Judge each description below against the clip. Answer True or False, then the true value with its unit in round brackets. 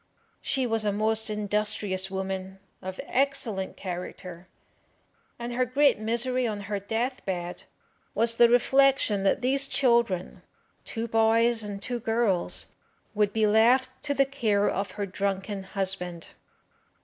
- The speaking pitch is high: True (215 Hz)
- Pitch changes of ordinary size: True (3.7 semitones)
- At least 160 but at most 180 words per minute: False (135 wpm)